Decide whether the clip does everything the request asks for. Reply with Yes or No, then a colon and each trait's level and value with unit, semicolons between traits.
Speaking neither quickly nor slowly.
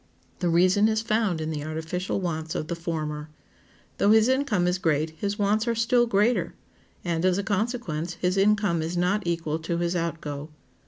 Yes: average, 180 wpm